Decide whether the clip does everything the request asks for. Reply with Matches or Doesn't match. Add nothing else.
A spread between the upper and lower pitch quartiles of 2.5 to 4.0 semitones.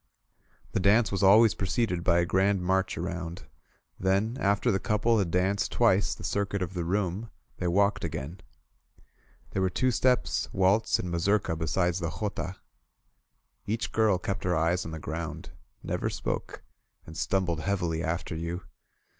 Matches